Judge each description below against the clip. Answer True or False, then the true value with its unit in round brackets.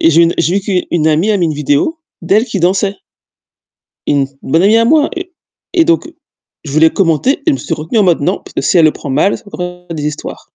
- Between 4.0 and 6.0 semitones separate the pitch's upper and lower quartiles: True (5.1 semitones)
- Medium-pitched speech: True (180 Hz)